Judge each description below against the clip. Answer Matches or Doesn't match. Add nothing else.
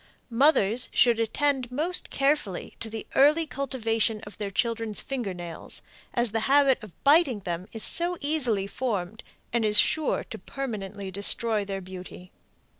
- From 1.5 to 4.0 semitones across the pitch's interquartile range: Doesn't match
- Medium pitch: Doesn't match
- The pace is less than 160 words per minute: Matches